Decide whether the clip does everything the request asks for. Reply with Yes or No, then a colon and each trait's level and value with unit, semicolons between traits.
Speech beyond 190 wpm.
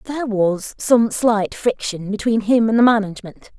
No: average, 170 wpm